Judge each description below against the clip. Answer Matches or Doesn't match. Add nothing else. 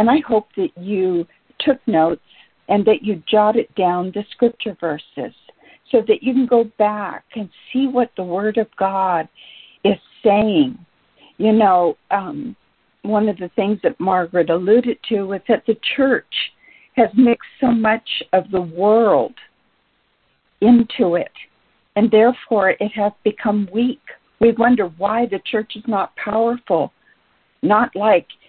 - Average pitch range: Matches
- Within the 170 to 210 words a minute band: Doesn't match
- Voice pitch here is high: Matches